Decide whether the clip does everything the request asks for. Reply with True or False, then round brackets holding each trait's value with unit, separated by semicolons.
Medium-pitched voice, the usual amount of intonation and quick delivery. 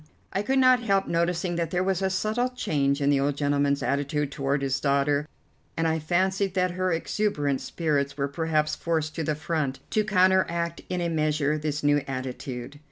False (155 Hz; 4.4 semitones; 185 wpm)